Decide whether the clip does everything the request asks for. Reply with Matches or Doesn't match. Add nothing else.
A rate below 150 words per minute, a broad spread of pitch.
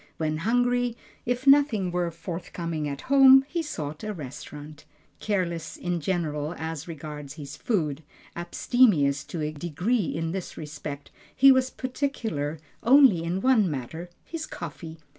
Matches